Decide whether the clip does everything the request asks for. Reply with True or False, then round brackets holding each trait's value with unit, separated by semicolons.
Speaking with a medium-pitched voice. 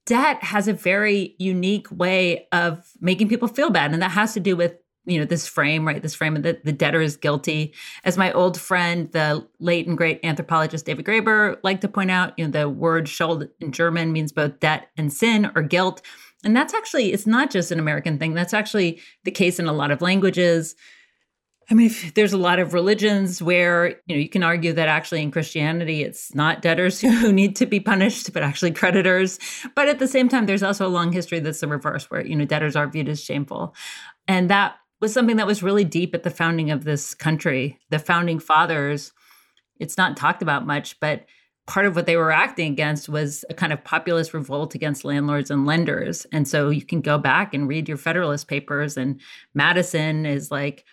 True (170 Hz)